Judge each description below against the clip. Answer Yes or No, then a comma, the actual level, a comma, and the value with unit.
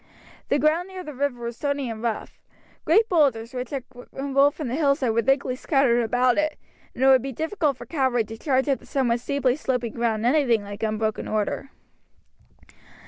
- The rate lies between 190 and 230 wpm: Yes, average, 195 wpm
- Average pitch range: Yes, average, 3.4 semitones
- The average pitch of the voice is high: Yes, very high, 260 Hz